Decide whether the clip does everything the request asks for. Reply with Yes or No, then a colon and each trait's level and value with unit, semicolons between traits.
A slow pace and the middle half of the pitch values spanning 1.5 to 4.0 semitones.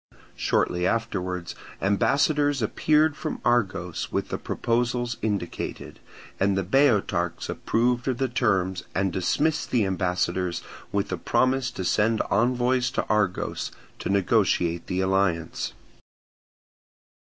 No: slow, 115 wpm; average, 4.9 semitones